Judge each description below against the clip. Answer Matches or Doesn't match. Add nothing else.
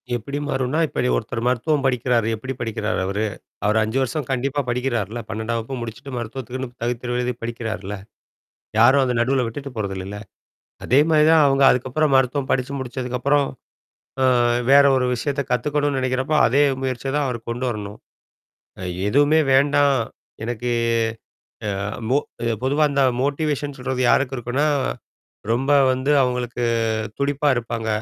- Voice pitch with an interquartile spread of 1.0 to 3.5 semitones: Matches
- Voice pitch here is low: Matches